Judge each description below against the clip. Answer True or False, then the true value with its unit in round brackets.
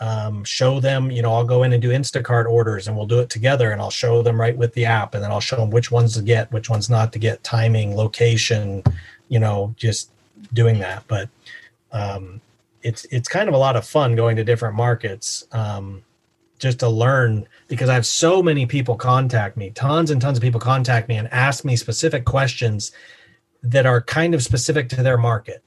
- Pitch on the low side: True (120 Hz)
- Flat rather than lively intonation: True (2.3 semitones)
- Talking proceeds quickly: True (215 wpm)